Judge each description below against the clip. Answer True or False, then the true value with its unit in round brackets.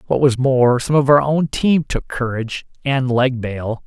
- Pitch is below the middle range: True (130 Hz)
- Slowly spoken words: False (200 wpm)